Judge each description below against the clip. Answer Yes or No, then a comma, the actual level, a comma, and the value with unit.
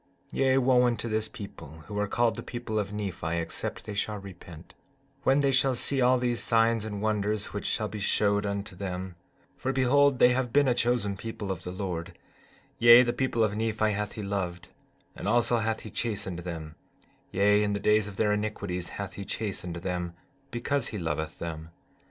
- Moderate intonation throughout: Yes, average, 3.8 semitones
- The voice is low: Yes, low, 105 Hz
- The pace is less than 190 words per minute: No, average, 195 wpm